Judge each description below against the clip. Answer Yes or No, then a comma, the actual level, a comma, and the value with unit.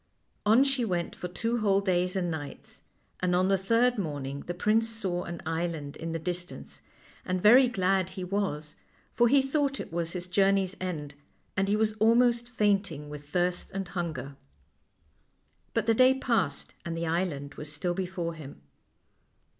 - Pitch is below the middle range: No, medium, 185 Hz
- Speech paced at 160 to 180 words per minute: Yes, average, 170 wpm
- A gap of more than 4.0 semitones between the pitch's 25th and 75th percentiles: Yes, average, 4.5 semitones